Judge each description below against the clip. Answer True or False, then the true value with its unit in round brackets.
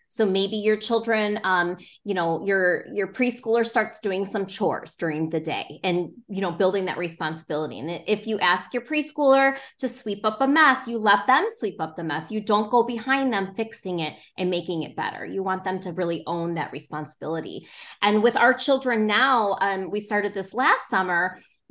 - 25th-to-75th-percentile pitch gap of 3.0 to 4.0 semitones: False (4.8 semitones)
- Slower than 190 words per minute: False (195 wpm)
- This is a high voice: True (200 Hz)